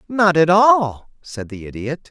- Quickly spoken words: No, average, 170 wpm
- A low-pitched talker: No, medium, 160 Hz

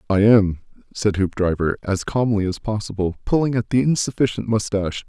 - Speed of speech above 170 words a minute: No, average, 155 wpm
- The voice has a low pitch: Yes, low, 105 Hz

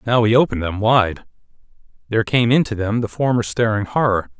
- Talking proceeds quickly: No, average, 175 wpm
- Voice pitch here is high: No, low, 110 Hz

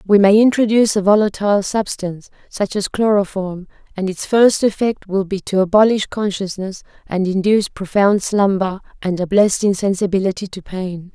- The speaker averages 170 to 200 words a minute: No, average, 150 wpm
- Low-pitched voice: No, high, 195 Hz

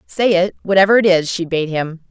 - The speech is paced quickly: Yes, fast, 230 wpm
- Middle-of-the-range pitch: Yes, medium, 180 Hz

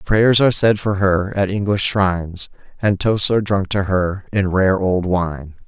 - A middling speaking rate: Yes, average, 190 wpm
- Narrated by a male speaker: Yes, male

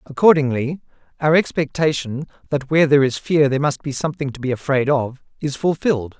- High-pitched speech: No, medium, 140 Hz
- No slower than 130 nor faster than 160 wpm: No, average, 175 wpm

